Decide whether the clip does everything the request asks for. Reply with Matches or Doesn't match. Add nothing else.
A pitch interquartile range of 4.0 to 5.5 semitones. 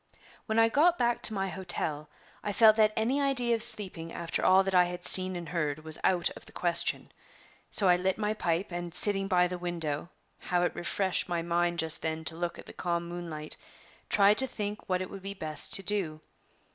Doesn't match